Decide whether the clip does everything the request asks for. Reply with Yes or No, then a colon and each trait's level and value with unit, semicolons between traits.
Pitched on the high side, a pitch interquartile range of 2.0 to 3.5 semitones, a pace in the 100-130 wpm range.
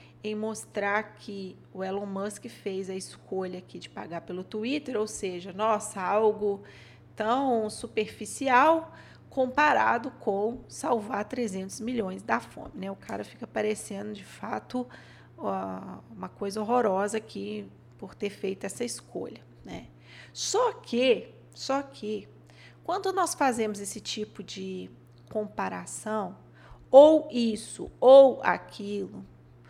No: high, 210 Hz; average, 3.9 semitones; slow, 120 wpm